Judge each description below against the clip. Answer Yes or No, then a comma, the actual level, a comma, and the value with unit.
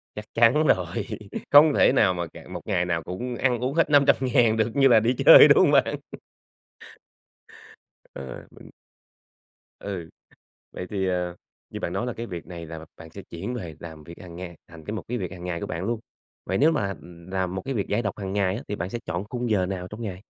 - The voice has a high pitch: No, very low, 95 Hz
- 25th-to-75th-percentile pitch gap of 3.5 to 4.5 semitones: No, average, 5.0 semitones